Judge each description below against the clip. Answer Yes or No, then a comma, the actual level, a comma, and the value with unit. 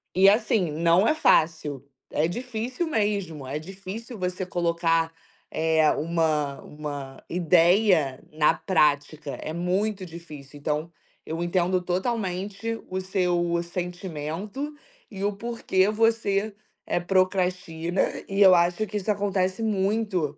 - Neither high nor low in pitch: Yes, medium, 180 Hz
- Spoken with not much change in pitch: No, average, 3.8 semitones